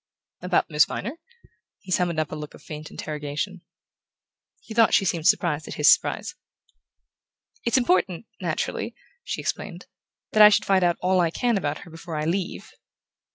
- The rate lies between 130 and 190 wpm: Yes, average, 165 wpm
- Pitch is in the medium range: Yes, medium, 175 Hz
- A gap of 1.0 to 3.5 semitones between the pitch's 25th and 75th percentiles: No, average, 4.0 semitones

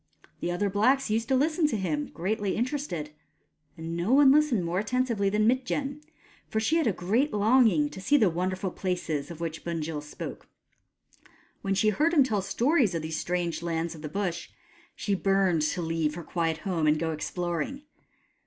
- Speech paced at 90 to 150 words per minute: No, average, 180 wpm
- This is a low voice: No, high, 190 Hz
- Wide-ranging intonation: Yes, wide, 6.6 semitones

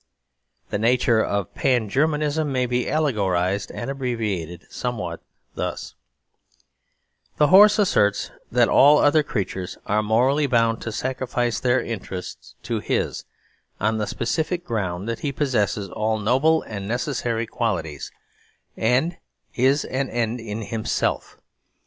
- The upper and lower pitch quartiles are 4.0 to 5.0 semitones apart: Yes, average, 4.5 semitones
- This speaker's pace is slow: Yes, slow, 125 wpm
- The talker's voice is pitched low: Yes, low, 115 Hz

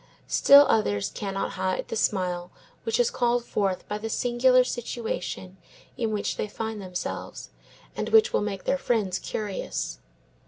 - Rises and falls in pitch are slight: No, average, 4.3 semitones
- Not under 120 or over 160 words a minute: Yes, average, 150 wpm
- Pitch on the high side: Yes, high, 210 Hz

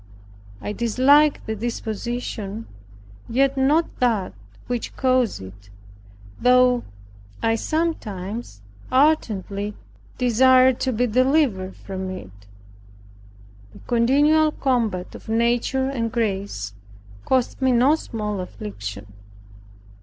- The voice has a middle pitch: No, high, 235 Hz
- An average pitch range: Yes, average, 4.6 semitones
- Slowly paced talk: Yes, slow, 95 wpm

